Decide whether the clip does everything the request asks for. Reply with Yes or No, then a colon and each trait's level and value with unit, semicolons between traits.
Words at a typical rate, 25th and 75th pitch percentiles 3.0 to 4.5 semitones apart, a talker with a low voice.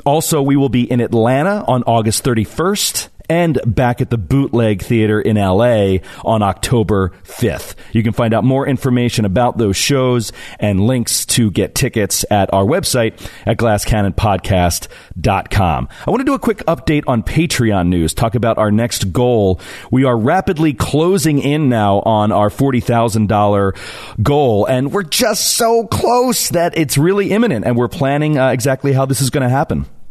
No: average, 165 wpm; average, 4.9 semitones; low, 120 Hz